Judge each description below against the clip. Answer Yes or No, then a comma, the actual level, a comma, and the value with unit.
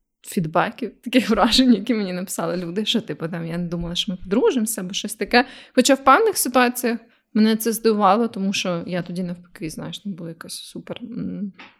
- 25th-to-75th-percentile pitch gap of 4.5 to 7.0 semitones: Yes, average, 4.9 semitones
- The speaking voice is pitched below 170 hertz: No, high, 215 Hz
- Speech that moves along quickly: Yes, fast, 185 wpm